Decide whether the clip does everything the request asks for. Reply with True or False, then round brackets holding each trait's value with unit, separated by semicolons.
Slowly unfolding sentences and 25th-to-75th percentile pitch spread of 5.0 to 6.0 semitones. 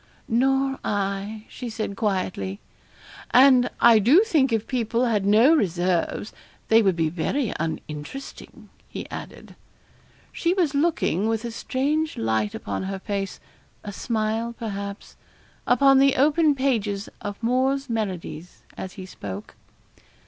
True (130 wpm; 5.5 semitones)